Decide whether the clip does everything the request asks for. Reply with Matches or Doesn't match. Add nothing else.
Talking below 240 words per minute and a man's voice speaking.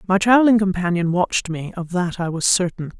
Doesn't match